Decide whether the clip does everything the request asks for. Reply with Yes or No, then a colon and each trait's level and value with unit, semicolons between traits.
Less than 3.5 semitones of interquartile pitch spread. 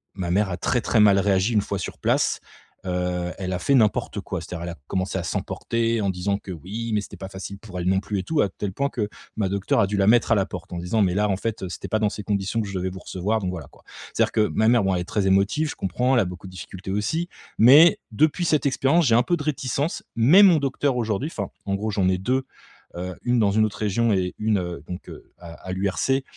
No: average, 3.8 semitones